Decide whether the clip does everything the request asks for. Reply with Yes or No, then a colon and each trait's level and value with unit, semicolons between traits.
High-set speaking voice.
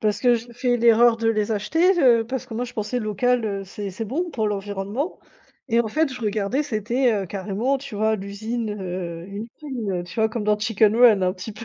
Yes: high, 220 Hz